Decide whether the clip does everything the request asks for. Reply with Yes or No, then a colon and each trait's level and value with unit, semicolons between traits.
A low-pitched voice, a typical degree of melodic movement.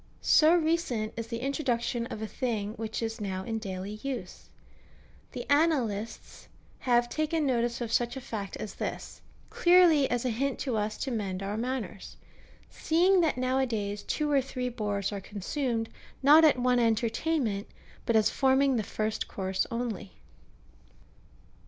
No: high, 235 Hz; average, 4.1 semitones